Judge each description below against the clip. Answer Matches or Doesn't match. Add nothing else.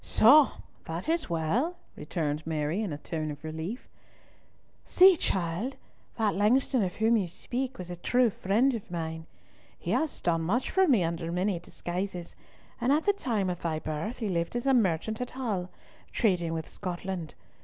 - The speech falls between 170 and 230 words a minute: Matches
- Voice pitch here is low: Doesn't match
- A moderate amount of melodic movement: Doesn't match